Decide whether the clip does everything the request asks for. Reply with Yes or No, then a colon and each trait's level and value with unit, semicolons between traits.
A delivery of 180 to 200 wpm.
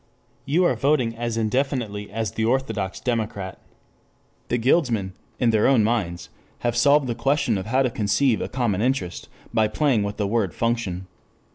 No: average, 170 wpm